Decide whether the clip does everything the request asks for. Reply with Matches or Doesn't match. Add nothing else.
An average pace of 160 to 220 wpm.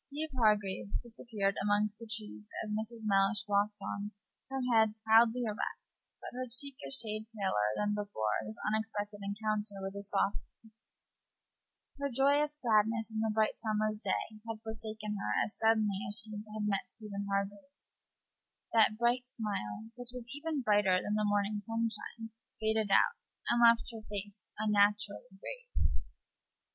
Doesn't match